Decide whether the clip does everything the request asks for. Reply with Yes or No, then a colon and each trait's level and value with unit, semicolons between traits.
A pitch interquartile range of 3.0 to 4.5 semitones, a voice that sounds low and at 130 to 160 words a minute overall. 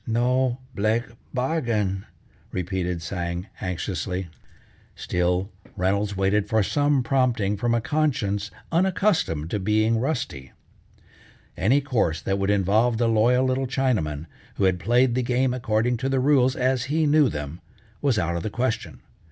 No: average, 5.1 semitones; low, 110 Hz; average, 145 wpm